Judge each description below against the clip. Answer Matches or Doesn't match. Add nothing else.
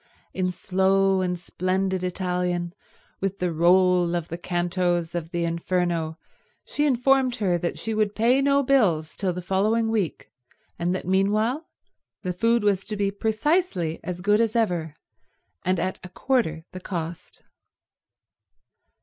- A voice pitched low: Doesn't match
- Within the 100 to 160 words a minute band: Matches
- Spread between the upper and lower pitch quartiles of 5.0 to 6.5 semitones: Doesn't match